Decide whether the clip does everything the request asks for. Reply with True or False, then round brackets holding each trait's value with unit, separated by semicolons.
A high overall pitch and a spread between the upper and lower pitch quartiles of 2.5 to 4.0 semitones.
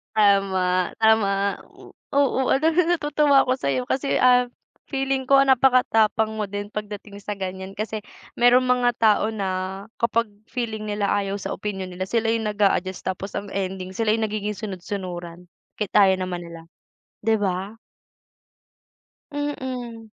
True (210 Hz; 3.7 semitones)